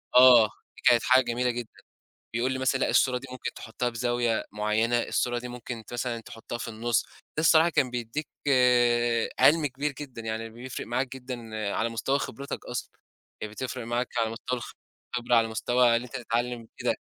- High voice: No, low, 120 Hz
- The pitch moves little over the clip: Yes, narrow, 1.8 semitones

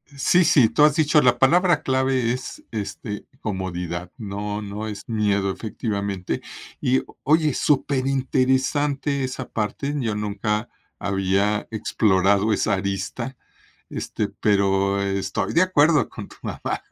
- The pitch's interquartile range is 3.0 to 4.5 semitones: No, average, 5.1 semitones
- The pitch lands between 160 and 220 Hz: No, low, 110 Hz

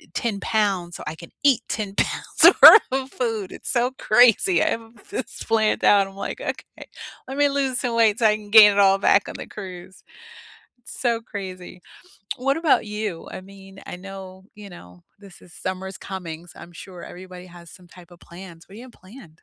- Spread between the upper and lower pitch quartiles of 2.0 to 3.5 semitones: No, average, 3.9 semitones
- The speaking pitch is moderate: No, high, 200 Hz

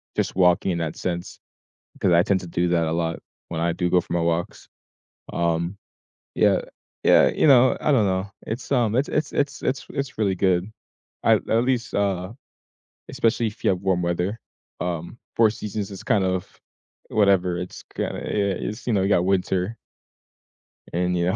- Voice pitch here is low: Yes, very low, 95 Hz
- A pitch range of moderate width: Yes, average, 3.7 semitones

